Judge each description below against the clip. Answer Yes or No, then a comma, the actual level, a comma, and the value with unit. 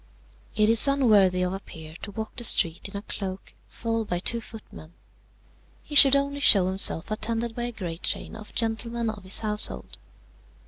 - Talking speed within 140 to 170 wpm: No, average, 180 wpm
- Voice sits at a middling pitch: No, high, 215 Hz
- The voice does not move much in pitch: No, average, 3.5 semitones